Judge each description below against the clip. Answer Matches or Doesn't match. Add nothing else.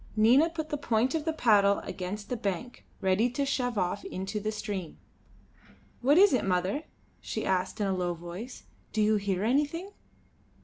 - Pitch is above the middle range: Matches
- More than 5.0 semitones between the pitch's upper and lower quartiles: Matches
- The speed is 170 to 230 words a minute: Matches